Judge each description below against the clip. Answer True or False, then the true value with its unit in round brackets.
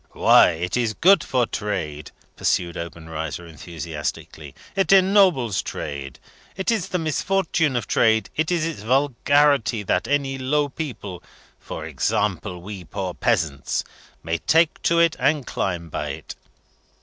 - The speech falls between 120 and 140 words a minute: True (135 wpm)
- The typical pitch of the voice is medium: False (115 Hz)